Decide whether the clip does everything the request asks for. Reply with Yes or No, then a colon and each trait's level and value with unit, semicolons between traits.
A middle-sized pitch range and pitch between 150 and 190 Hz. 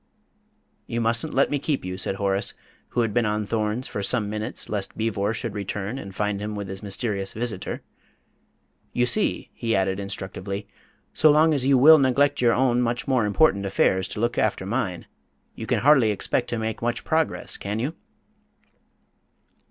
No: average, 3.9 semitones; low, 110 Hz